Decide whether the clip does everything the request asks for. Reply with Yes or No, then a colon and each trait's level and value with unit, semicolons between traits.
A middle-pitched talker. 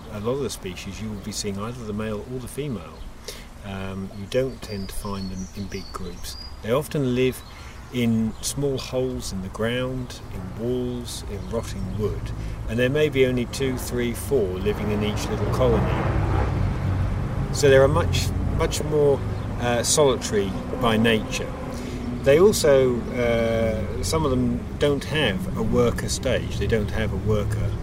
No: low, 110 Hz